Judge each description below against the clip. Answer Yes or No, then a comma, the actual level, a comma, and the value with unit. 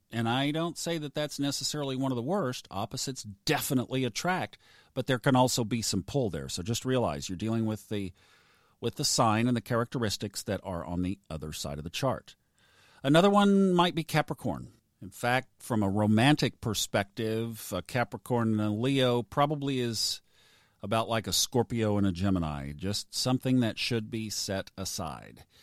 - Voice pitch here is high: No, low, 115 Hz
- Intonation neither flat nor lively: Yes, average, 4.6 semitones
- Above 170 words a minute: Yes, average, 180 wpm